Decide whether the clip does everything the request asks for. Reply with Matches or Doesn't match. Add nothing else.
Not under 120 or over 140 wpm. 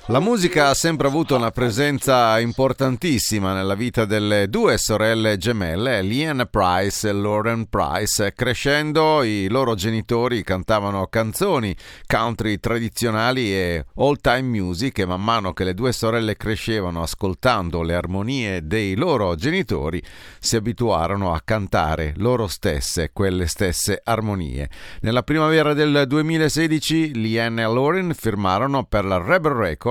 Matches